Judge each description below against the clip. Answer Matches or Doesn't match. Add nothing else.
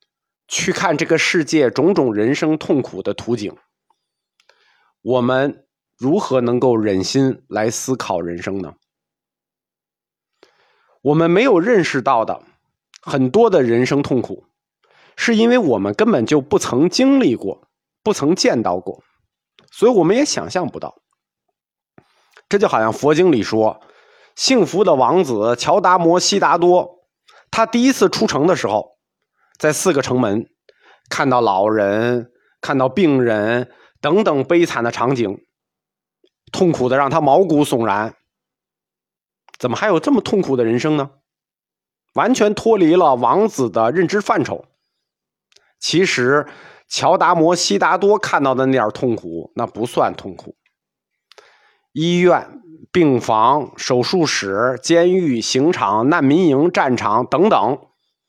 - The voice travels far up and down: Matches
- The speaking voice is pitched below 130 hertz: Doesn't match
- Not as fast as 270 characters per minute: Matches